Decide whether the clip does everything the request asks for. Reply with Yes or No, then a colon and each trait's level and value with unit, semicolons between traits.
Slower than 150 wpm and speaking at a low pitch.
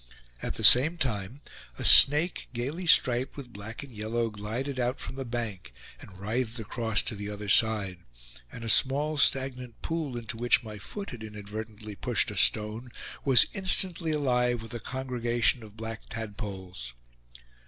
No: average, 160 wpm; low, 120 Hz